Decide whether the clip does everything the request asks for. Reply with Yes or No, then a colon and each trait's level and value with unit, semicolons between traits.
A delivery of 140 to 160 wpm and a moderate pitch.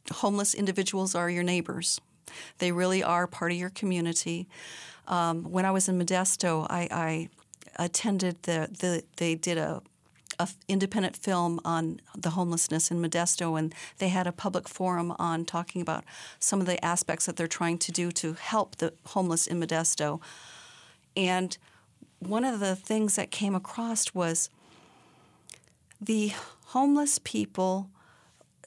Yes: average, 145 wpm; medium, 175 Hz